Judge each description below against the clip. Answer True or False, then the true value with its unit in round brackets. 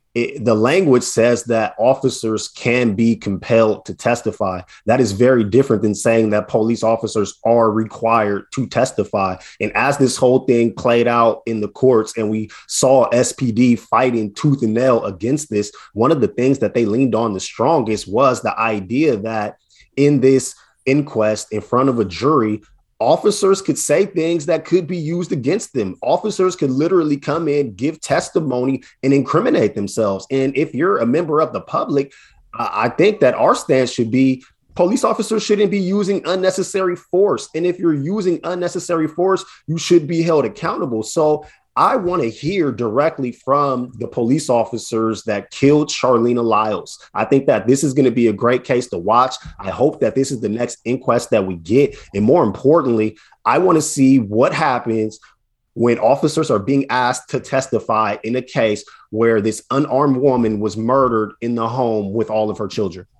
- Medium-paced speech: True (180 wpm)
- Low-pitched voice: True (125 Hz)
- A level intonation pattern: False (4.8 semitones)